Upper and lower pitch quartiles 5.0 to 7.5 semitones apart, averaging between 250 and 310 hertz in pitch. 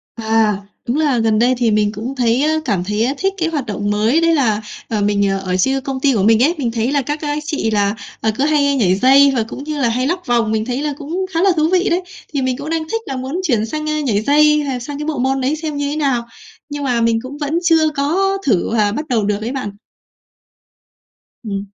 Yes: average, 5.3 semitones; very high, 265 Hz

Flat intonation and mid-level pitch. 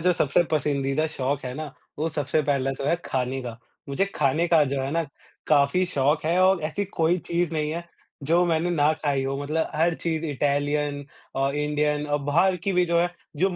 No: average, 3.0 semitones; medium, 150 Hz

